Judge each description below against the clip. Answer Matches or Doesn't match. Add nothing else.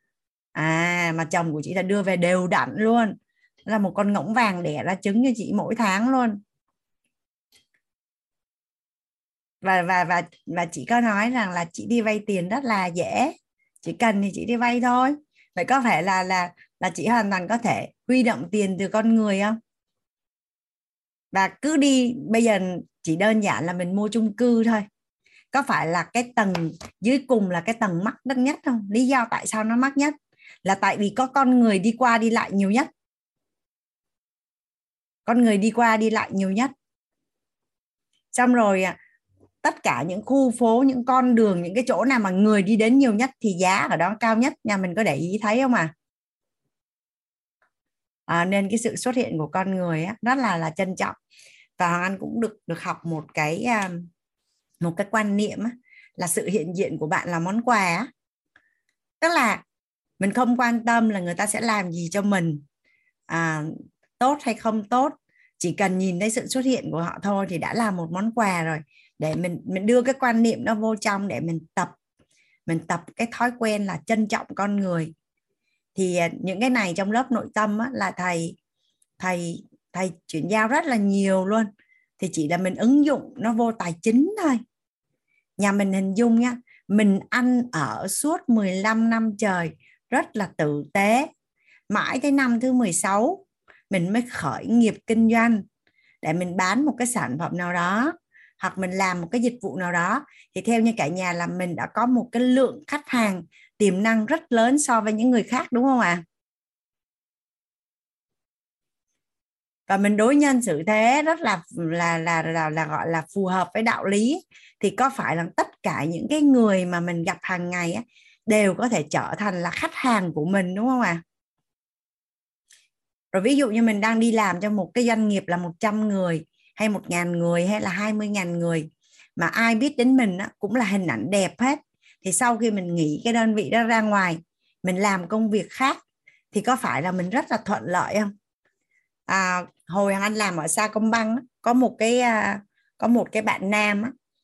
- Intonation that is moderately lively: Matches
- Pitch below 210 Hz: Doesn't match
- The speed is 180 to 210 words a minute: Matches